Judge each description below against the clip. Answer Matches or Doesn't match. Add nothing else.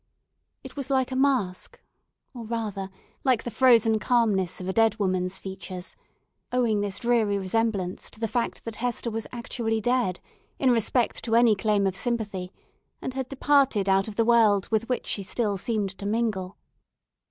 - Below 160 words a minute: Doesn't match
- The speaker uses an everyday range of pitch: Matches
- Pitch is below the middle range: Doesn't match